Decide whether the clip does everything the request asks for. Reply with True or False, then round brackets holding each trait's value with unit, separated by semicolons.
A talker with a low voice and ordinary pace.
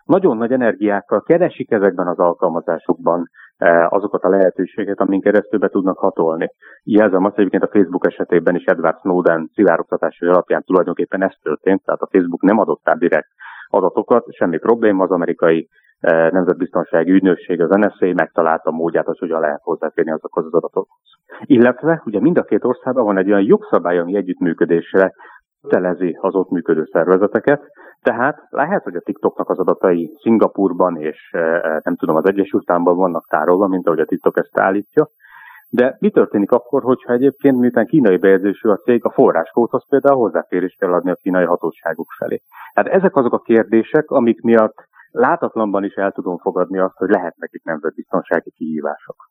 False (100 Hz; 165 wpm)